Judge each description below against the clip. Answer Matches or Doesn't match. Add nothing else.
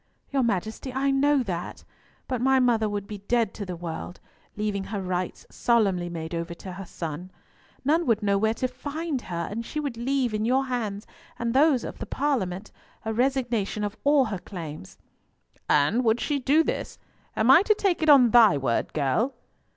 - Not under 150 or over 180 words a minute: Doesn't match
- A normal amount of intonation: Doesn't match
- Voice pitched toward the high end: Matches